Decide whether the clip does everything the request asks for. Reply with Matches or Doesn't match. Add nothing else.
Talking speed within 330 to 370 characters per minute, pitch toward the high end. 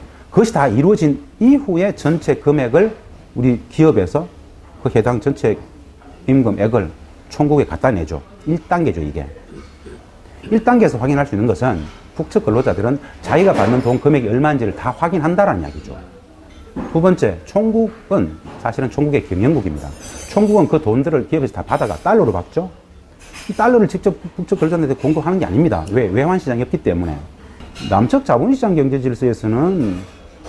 Doesn't match